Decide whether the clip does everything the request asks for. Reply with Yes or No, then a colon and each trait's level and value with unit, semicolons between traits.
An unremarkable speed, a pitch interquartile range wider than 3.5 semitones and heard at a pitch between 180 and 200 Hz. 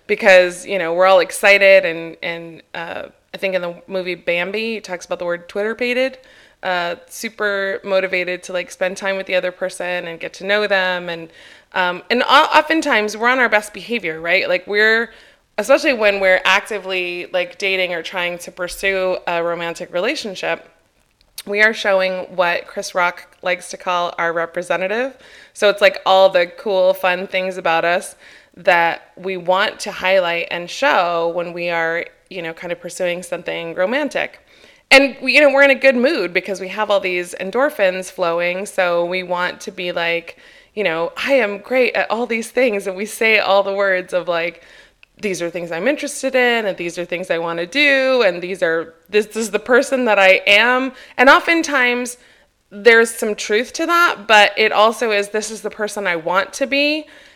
Yes: average, 190 wpm; average, 3.9 semitones; high, 190 Hz